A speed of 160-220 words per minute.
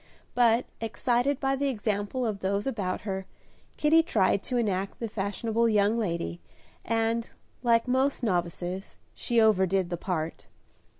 No: slow, 135 wpm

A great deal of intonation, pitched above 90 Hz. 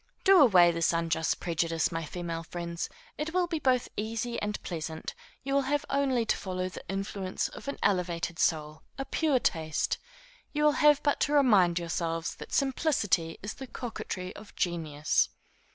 Yes: wide, 8.2 semitones; high, 190 Hz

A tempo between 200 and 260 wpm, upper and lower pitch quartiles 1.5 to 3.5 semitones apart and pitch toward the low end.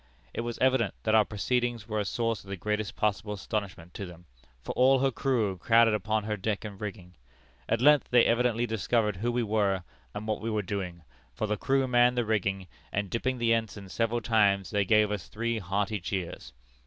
Yes: fast, 205 wpm; average, 2.9 semitones; low, 110 Hz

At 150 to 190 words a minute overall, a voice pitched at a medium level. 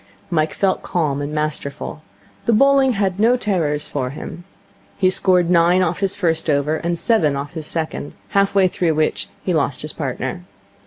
Yes: average, 175 wpm; medium, 170 Hz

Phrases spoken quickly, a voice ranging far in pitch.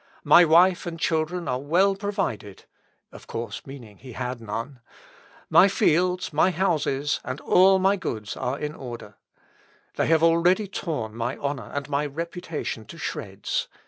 No: average, 150 wpm; wide, 6.1 semitones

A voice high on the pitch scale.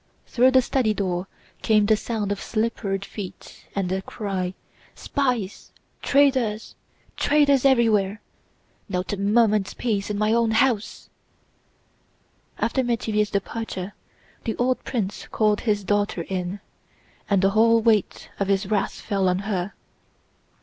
Yes: high, 210 Hz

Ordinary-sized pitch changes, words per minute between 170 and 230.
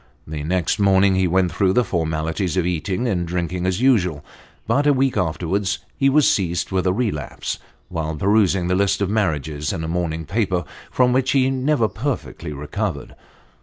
Yes: average, 4.9 semitones; average, 175 wpm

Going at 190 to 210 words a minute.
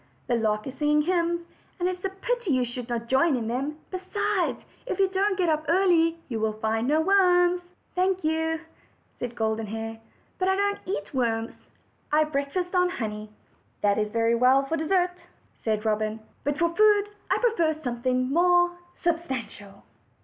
No: average, 170 wpm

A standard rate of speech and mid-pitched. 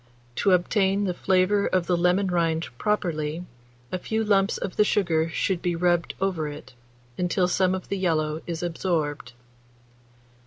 Yes: average, 155 wpm; medium, 180 Hz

